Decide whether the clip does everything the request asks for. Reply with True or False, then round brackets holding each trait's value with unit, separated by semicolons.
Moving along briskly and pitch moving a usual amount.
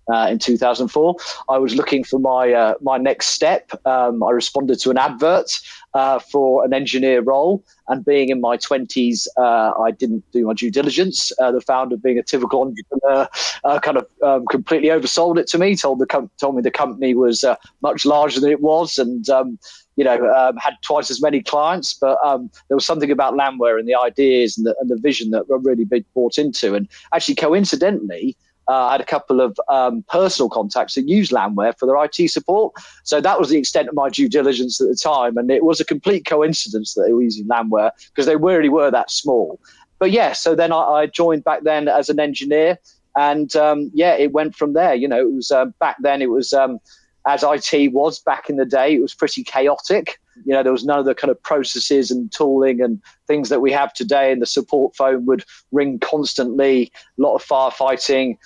True (220 wpm; 3.0 semitones)